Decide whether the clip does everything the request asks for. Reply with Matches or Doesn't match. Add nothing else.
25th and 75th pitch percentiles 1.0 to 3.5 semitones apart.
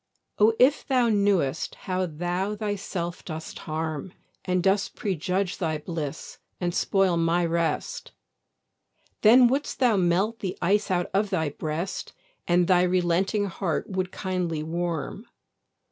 Matches